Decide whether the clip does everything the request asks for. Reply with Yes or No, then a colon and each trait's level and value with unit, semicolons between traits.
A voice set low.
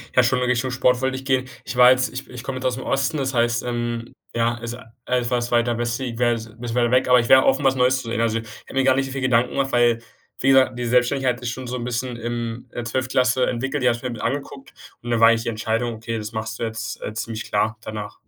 Yes: low, 120 Hz